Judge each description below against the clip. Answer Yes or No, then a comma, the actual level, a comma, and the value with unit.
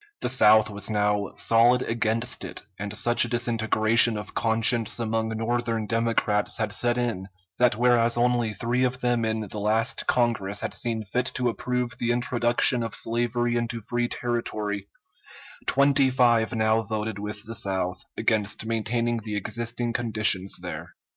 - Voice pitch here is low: Yes, low, 115 Hz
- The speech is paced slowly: No, average, 155 wpm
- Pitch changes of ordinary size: No, narrow, 1.9 semitones